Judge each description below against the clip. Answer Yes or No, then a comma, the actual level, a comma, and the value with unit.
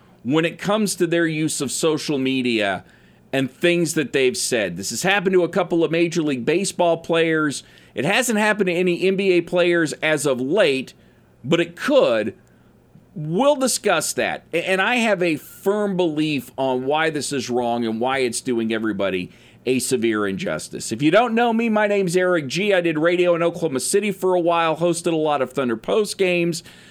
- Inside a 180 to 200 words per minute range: Yes, average, 190 wpm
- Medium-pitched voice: Yes, medium, 170 Hz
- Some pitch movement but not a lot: No, wide, 5.7 semitones